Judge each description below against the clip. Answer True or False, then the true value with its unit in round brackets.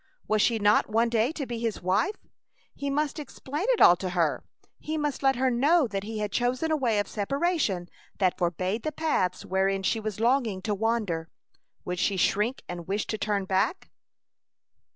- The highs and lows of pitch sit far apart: True (5.8 semitones)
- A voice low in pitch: False (220 Hz)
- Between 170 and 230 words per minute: True (190 wpm)